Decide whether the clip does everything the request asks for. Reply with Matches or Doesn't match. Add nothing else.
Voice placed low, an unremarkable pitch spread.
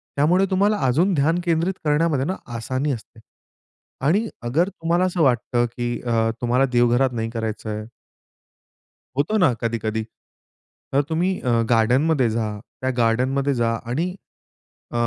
Doesn't match